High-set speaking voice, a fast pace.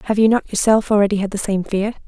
Yes: high, 205 Hz; fast, 260 wpm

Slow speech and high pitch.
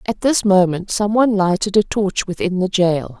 No: fast, 205 wpm; high, 195 Hz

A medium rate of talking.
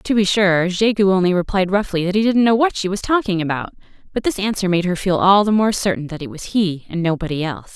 No: fast, 255 wpm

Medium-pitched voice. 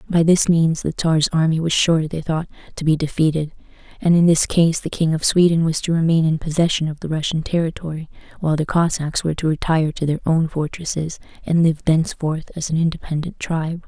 Yes: medium, 160 Hz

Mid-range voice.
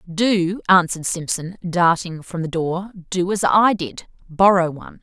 Yes: medium, 180 Hz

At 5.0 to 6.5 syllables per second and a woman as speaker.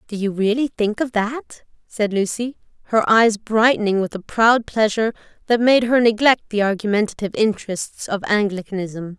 Yes: 5.1 syllables/s; female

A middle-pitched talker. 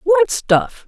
No: very high, 275 Hz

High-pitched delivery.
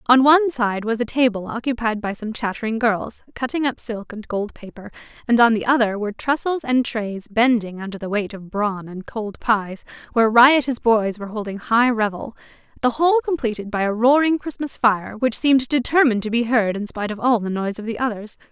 Yes: high, 230 Hz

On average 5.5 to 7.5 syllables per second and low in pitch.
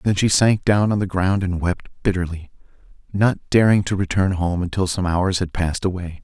No: 5.3 syllables/s; very low, 95 Hz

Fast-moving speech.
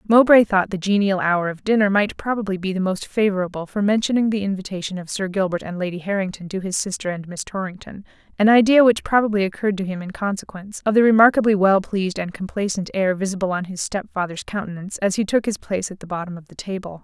Yes: fast, 220 wpm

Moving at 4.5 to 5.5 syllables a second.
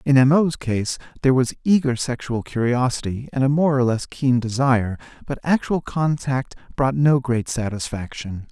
Yes: 4.8 syllables/s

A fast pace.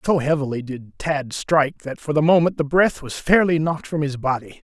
Yes: fast, 215 wpm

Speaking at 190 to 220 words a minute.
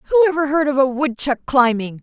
Yes: fast, 205 wpm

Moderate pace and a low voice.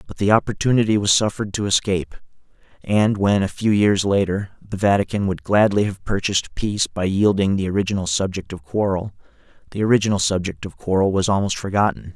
Yes: average, 175 wpm; low, 100 Hz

